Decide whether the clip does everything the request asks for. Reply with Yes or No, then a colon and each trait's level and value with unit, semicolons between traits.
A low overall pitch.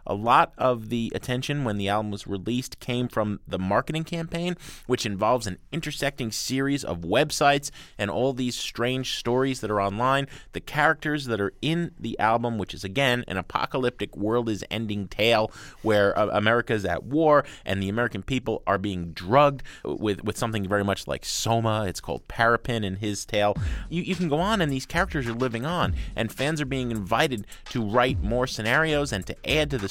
Yes: low, 120 Hz